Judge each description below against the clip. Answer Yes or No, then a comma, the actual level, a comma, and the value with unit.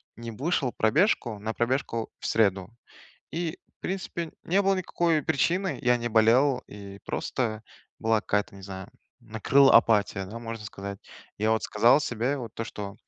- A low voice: Yes, low, 115 Hz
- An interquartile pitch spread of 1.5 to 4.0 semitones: No, average, 4.7 semitones